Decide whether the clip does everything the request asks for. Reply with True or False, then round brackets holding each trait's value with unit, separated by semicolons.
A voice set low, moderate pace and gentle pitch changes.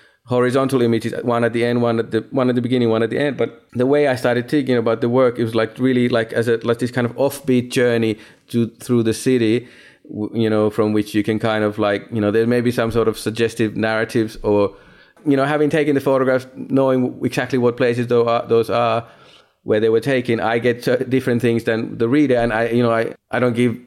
False (120 Hz; 240 wpm; 1.9 semitones)